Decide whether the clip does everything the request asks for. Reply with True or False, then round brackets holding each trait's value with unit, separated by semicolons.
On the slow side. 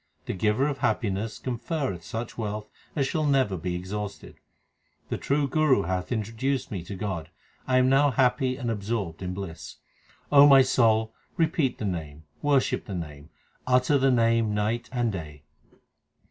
False (160 wpm)